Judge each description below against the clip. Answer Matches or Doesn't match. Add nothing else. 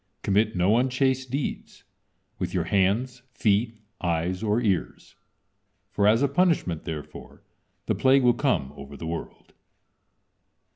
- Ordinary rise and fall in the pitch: Doesn't match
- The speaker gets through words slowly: Matches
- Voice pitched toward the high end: Doesn't match